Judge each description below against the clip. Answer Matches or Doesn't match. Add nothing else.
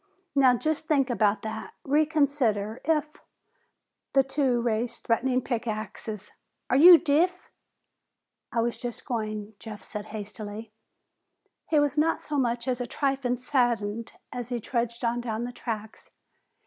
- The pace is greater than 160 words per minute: Doesn't match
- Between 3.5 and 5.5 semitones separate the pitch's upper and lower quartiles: Matches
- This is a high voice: Matches